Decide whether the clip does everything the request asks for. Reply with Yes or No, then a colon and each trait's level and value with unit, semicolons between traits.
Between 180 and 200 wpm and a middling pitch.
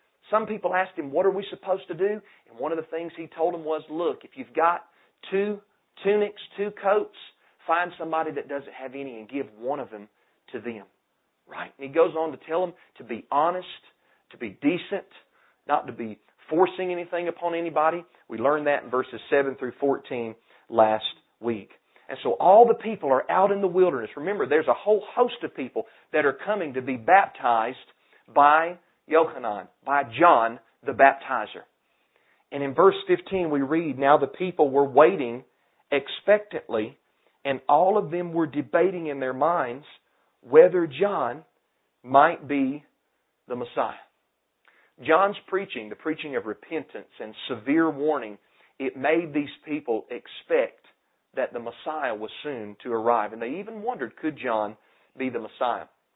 No: average, 170 wpm; medium, 160 Hz